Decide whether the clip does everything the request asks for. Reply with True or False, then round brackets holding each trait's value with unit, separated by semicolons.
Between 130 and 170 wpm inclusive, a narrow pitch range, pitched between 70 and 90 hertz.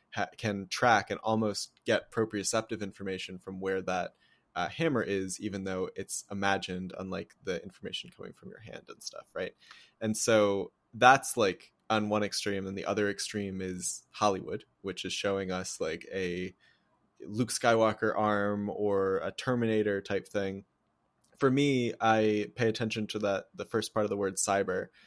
False (165 wpm; 2.3 semitones; 100 Hz)